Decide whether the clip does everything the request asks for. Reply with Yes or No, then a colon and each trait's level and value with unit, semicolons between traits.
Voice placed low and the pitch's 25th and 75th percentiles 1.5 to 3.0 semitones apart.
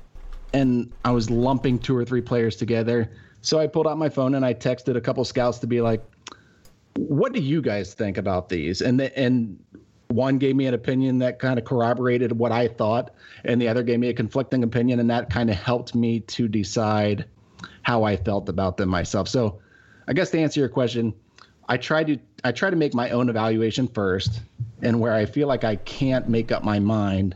Yes: low, 120 Hz; average, 2.7 semitones